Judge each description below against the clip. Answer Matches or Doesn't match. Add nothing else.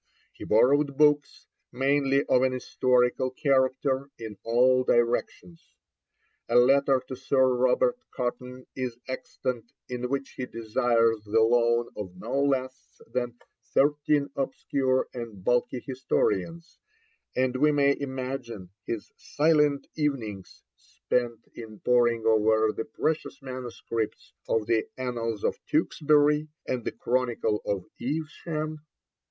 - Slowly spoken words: Matches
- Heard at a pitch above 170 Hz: Doesn't match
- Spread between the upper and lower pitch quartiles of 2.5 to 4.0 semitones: Matches